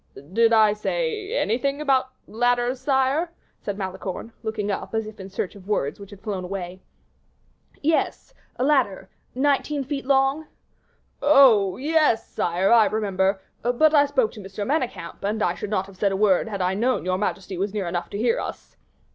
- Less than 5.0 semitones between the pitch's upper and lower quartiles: No, wide, 5.6 semitones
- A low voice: No, high, 220 Hz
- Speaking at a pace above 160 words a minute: Yes, average, 180 wpm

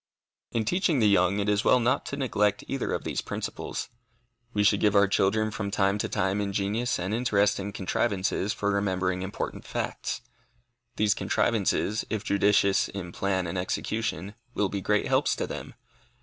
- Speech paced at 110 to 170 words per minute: Yes, average, 165 wpm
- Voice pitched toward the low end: Yes, low, 100 Hz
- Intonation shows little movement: Yes, narrow, 1.8 semitones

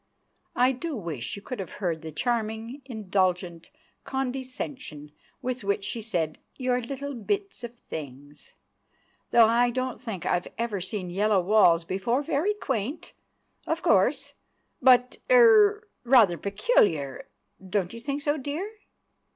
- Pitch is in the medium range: No, high, 230 Hz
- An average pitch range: No, wide, 6.3 semitones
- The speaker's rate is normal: No, slow, 125 wpm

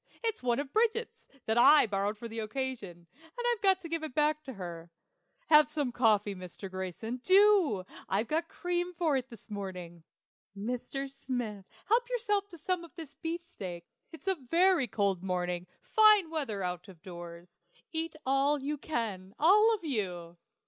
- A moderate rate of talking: Yes, average, 170 wpm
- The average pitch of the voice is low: No, very high, 260 Hz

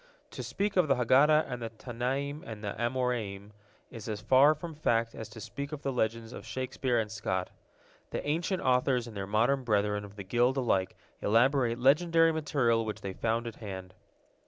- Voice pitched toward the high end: No, low, 120 Hz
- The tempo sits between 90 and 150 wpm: No, average, 180 wpm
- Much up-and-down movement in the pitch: No, average, 4.1 semitones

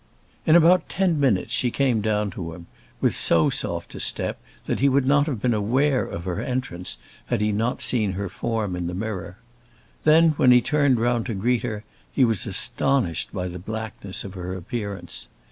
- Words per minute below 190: No, average, 195 wpm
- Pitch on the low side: Yes, low, 110 Hz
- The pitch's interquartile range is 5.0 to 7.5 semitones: Yes, wide, 5.5 semitones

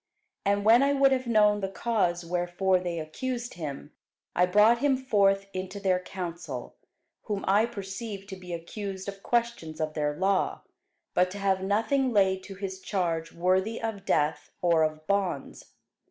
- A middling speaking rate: Yes, average, 165 wpm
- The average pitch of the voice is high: Yes, high, 195 Hz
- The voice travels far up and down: No, average, 3.3 semitones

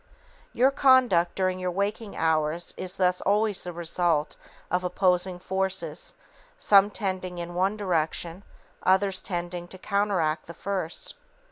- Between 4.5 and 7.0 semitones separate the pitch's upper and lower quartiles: No, narrow, 2.4 semitones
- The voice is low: No, medium, 185 Hz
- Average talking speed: No, slow, 130 wpm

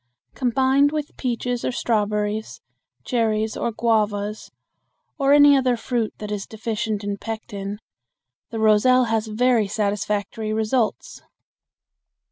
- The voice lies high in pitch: Yes, high, 220 Hz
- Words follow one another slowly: Yes, slow, 110 wpm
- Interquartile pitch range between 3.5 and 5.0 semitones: No, average, 2.8 semitones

